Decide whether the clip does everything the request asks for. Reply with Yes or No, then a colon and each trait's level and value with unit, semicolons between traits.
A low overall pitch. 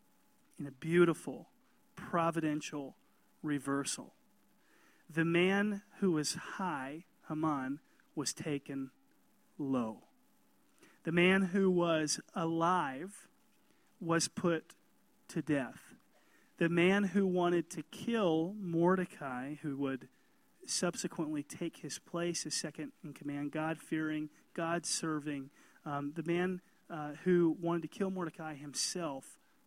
No: medium, 165 Hz